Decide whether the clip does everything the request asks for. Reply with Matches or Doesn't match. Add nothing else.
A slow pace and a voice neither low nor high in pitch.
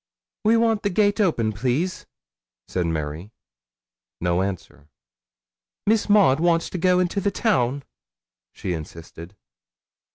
Matches